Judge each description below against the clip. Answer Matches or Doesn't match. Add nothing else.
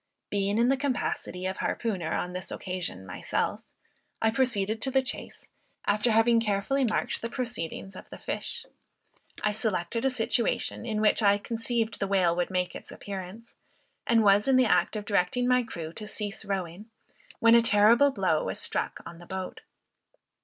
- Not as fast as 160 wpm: Doesn't match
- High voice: Matches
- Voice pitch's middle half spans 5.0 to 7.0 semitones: Doesn't match